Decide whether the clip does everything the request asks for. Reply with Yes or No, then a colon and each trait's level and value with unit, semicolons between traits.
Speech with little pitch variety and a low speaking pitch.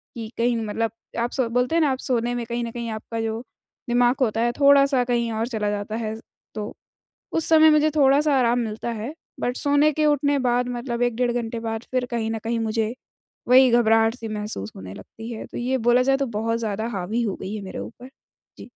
No: narrow, 2.3 semitones; high, 235 Hz